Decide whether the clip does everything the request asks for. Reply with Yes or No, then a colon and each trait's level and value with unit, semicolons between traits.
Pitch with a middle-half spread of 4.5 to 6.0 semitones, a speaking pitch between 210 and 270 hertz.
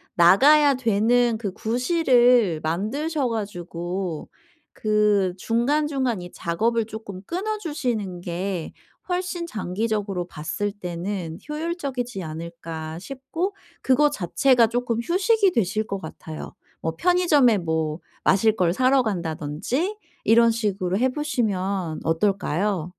No: wide, 6.6 semitones; high, 215 Hz